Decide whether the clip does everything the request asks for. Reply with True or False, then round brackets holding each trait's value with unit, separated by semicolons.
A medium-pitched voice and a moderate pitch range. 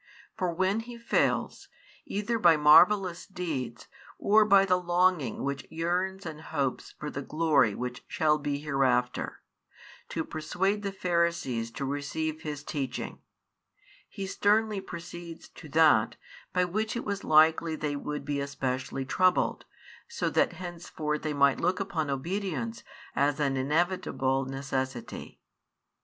True (160 Hz; 4.8 semitones)